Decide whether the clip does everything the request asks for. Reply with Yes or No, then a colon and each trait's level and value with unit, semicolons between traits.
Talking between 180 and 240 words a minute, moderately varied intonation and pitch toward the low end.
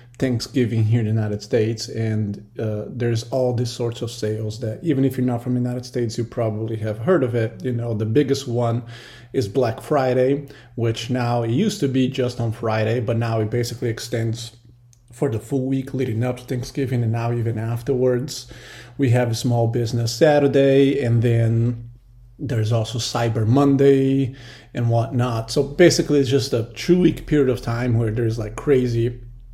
No: average, 185 wpm; narrow, 2.2 semitones; low, 120 Hz